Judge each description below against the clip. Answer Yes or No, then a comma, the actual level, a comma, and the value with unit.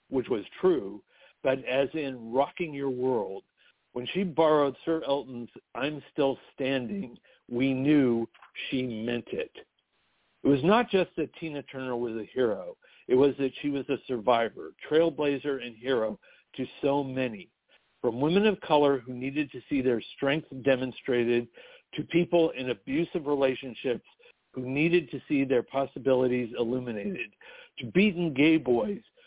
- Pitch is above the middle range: No, medium, 140 Hz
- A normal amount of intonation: Yes, average, 4.2 semitones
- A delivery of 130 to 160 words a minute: Yes, average, 150 wpm